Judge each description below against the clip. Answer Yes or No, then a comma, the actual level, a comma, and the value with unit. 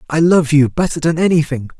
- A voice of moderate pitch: Yes, medium, 155 Hz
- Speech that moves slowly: No, average, 200 wpm